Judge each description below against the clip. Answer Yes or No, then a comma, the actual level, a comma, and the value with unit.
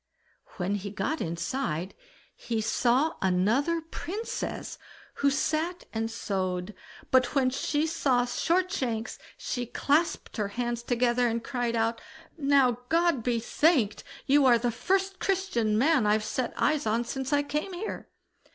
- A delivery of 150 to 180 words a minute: No, average, 140 wpm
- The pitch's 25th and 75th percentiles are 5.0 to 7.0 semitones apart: Yes, wide, 5.4 semitones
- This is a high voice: Yes, high, 245 Hz